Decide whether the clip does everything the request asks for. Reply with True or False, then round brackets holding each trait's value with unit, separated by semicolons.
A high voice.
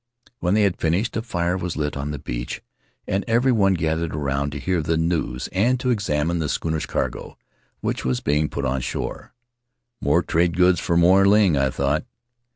False (85 Hz)